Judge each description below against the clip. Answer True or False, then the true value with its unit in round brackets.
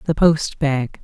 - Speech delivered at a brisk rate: False (175 wpm)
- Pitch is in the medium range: True (150 Hz)